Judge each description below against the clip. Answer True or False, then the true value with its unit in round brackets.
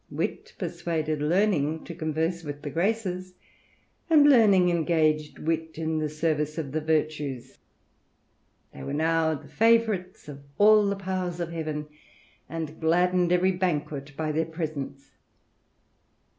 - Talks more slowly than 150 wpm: True (140 wpm)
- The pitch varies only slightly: False (3.0 semitones)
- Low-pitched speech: False (160 Hz)